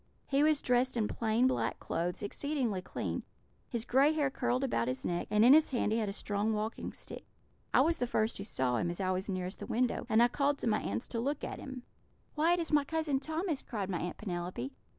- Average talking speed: No, fast, 235 wpm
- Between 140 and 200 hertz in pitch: No, high, 235 Hz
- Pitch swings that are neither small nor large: No, wide, 6.0 semitones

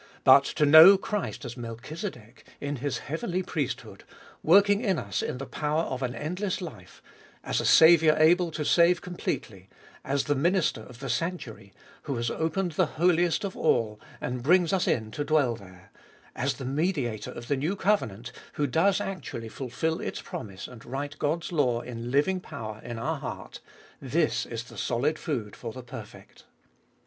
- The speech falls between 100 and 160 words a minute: No, average, 175 wpm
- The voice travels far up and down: Yes, wide, 6.2 semitones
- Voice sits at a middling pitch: Yes, medium, 145 Hz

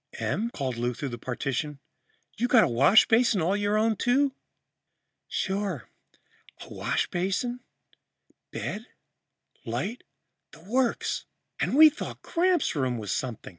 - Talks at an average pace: No, slow, 120 wpm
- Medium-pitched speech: No, high, 200 Hz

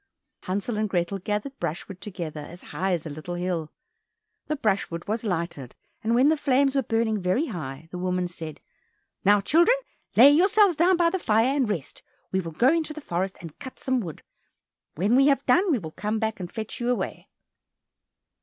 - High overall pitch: Yes, high, 210 Hz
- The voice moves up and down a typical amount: No, wide, 7.6 semitones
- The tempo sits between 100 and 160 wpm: No, average, 190 wpm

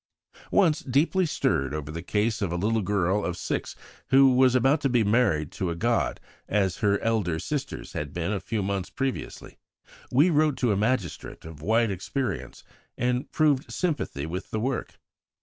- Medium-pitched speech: No, low, 110 Hz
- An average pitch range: No, wide, 6.3 semitones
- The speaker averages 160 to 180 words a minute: Yes, average, 175 wpm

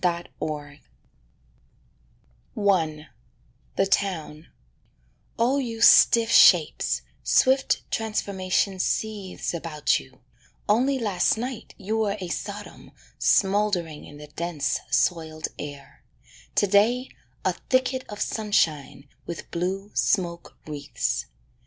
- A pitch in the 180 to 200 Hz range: Yes, high, 190 Hz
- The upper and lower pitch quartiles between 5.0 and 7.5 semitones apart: Yes, wide, 5.5 semitones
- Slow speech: Yes, slow, 100 wpm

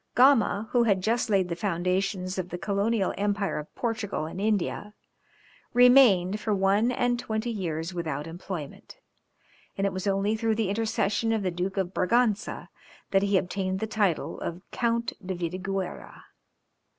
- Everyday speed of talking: Yes, average, 155 wpm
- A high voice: Yes, high, 195 Hz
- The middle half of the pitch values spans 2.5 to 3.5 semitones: Yes, average, 3.2 semitones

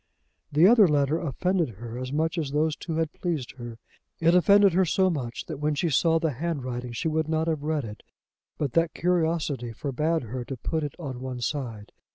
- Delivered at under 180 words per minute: No, fast, 205 wpm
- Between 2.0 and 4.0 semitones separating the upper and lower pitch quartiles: No, average, 4.4 semitones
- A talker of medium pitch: Yes, medium, 150 Hz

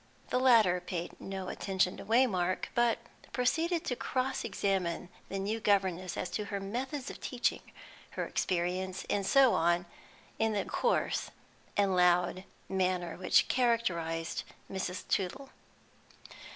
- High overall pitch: Yes, high, 195 Hz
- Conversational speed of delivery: No, slow, 130 wpm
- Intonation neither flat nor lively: Yes, average, 4.7 semitones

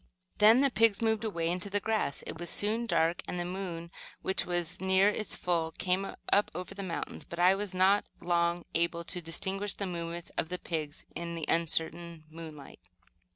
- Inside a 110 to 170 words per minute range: No, average, 190 wpm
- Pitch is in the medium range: Yes, medium, 180 Hz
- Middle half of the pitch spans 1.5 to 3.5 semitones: Yes, average, 2.8 semitones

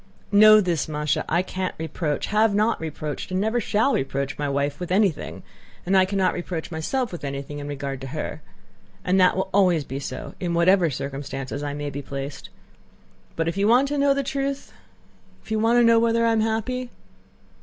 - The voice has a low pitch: No, medium, 180 Hz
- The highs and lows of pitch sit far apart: Yes, wide, 7.1 semitones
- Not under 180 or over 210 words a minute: Yes, average, 195 wpm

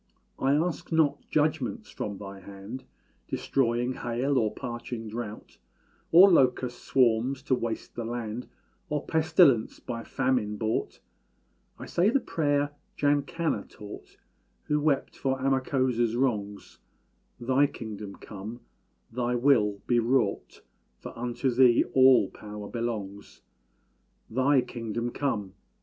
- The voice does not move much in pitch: No, average, 3.6 semitones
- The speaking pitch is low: Yes, low, 120 Hz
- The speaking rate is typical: No, slow, 120 wpm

